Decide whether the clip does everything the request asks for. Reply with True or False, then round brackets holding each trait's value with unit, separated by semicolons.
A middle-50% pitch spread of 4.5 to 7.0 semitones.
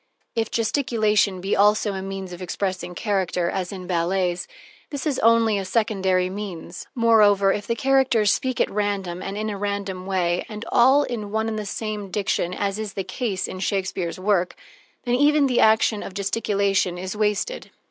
False (2.7 semitones)